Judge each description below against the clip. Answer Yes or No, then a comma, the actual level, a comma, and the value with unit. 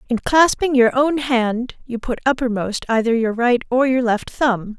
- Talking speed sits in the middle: Yes, average, 190 wpm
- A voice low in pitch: No, high, 245 Hz